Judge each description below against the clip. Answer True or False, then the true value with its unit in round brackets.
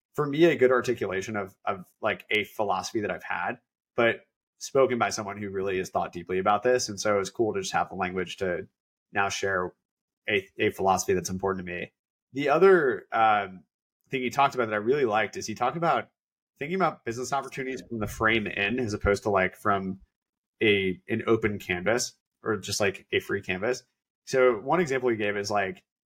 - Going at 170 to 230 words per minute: True (205 wpm)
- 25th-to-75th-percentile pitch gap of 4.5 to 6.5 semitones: True (4.8 semitones)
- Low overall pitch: True (110 Hz)